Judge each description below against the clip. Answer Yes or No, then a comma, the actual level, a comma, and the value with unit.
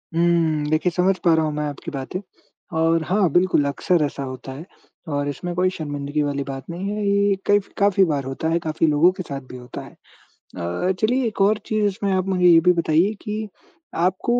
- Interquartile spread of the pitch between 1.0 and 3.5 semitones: No, average, 4.7 semitones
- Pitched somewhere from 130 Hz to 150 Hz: No, medium, 170 Hz